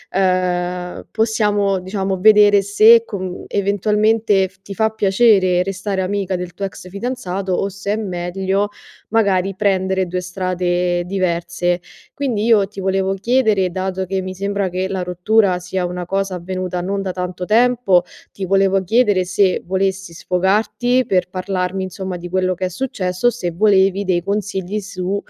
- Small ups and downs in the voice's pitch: Yes, narrow, 1.9 semitones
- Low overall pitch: No, high, 190 Hz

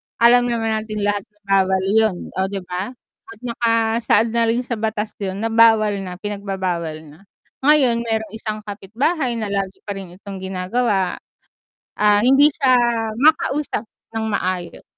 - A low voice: No, high, 215 Hz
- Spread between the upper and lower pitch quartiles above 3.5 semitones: No, average, 3.2 semitones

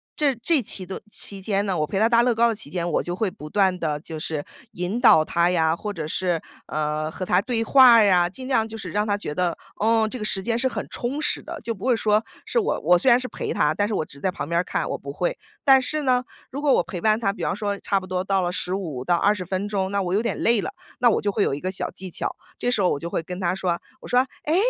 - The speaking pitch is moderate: No, high, 200 Hz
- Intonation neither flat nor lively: Yes, average, 4.6 semitones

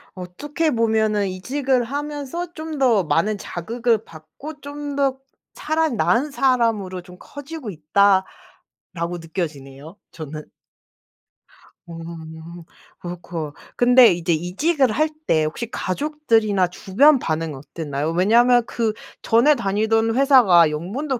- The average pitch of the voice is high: Yes, high, 215 Hz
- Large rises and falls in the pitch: Yes, wide, 8.0 semitones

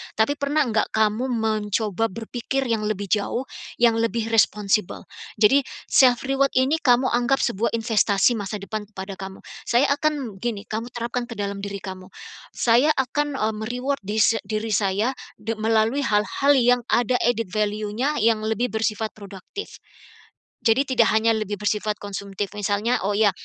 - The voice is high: Yes, high, 225 Hz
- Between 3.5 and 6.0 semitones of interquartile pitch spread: No, average, 3.0 semitones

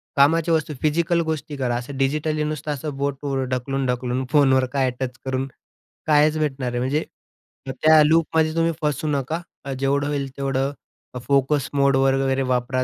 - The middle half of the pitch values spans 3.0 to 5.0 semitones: No, narrow, 2.5 semitones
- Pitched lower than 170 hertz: Yes, medium, 140 Hz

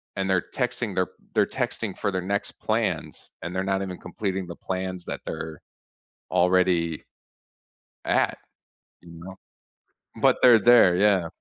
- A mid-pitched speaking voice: No, very low, 95 Hz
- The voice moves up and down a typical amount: No, narrow, 1.9 semitones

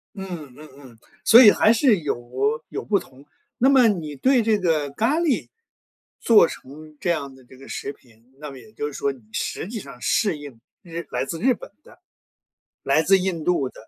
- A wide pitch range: Yes, wide, 7.5 semitones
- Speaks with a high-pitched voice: No, medium, 165 Hz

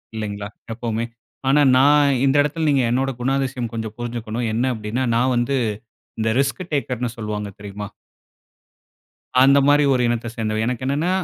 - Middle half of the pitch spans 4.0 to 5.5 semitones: No, average, 3.4 semitones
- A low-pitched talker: Yes, low, 120 Hz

